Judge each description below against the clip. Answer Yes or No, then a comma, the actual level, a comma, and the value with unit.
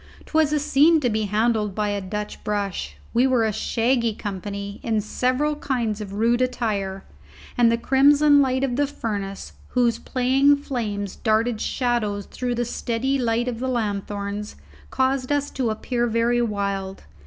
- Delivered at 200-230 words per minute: No, average, 160 wpm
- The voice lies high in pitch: Yes, high, 235 Hz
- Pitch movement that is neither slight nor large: Yes, average, 3.8 semitones